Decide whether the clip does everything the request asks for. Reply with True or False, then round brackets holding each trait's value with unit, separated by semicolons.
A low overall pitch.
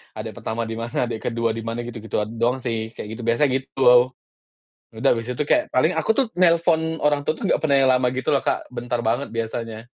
True (120 Hz)